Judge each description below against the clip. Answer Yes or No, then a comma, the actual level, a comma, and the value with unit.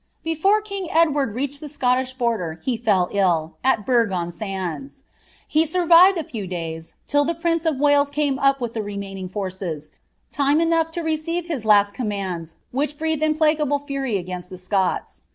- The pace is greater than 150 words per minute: Yes, average, 170 wpm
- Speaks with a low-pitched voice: No, very high, 260 Hz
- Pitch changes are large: Yes, wide, 8.0 semitones